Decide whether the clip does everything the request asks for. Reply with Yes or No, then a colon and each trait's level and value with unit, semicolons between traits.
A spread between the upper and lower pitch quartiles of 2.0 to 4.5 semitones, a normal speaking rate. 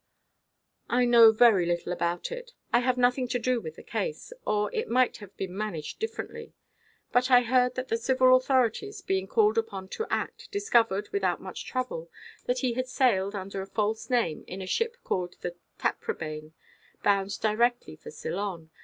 No: average, 4.9 semitones; average, 175 wpm